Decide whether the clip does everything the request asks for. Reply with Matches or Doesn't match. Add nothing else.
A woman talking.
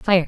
Matches